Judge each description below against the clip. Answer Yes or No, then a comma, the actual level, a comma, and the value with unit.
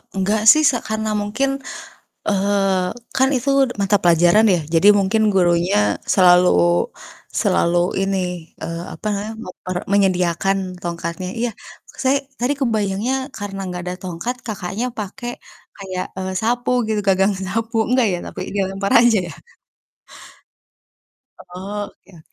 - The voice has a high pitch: Yes, high, 195 Hz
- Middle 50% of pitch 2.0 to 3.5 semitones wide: Yes, average, 3.1 semitones